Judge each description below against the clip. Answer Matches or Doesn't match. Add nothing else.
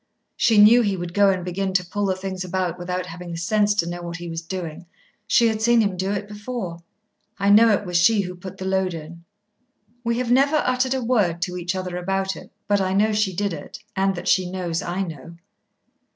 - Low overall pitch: Doesn't match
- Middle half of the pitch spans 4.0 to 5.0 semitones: Doesn't match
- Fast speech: Matches